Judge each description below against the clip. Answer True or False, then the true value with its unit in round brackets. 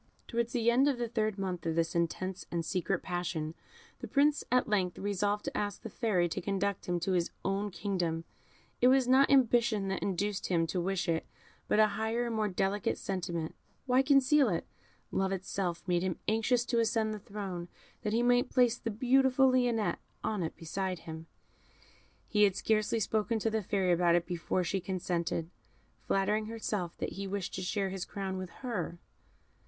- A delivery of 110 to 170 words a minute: False (185 wpm)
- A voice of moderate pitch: False (200 Hz)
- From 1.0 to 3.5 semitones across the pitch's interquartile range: False (4.1 semitones)